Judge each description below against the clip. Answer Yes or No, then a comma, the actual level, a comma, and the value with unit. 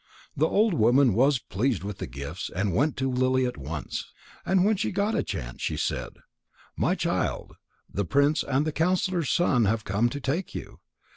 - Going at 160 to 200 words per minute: Yes, average, 190 wpm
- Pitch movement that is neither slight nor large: No, wide, 7.3 semitones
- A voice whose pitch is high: No, low, 130 Hz